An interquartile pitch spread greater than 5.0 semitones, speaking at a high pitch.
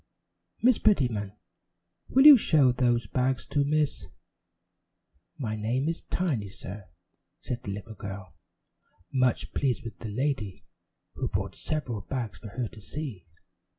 No: wide, 5.5 semitones; low, 120 Hz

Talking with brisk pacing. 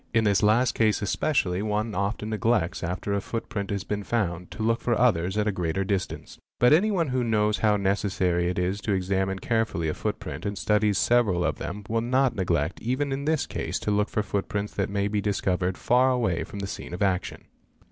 Yes: fast, 210 wpm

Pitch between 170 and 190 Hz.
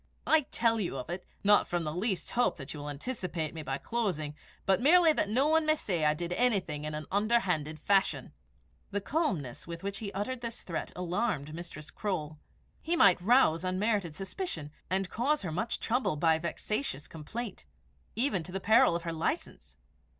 Yes: medium, 185 Hz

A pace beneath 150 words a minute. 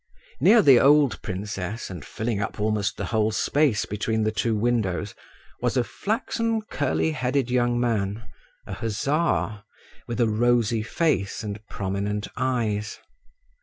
Yes: slow, 135 wpm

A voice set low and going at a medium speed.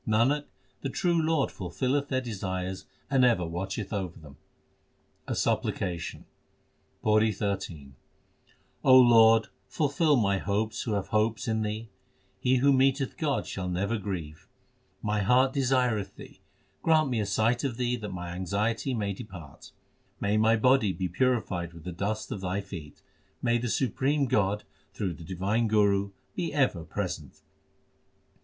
Yes: low, 110 Hz; average, 145 wpm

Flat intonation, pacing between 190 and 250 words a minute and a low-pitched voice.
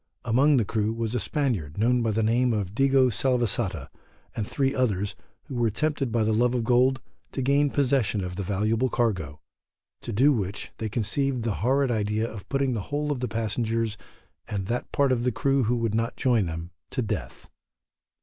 No: average, 3.5 semitones; average, 195 wpm; low, 115 Hz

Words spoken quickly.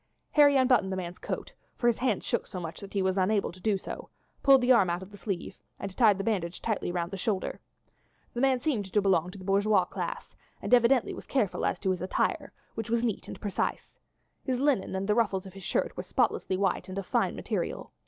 Yes: fast, 230 wpm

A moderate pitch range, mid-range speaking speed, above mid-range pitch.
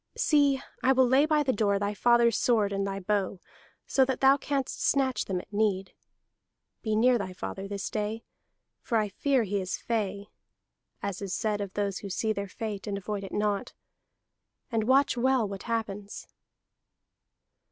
Yes: average, 3.8 semitones; average, 175 wpm; high, 210 Hz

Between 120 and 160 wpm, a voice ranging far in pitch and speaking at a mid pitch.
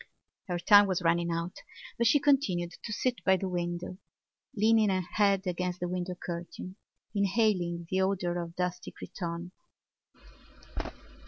No: average, 140 wpm; narrow, 2.4 semitones; medium, 180 Hz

